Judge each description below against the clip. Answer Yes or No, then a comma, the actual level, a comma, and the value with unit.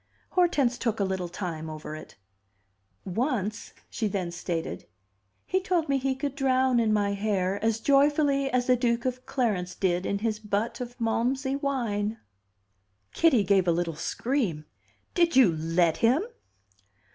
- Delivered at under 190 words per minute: Yes, average, 150 wpm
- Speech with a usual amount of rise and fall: No, wide, 5.8 semitones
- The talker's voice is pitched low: No, high, 225 Hz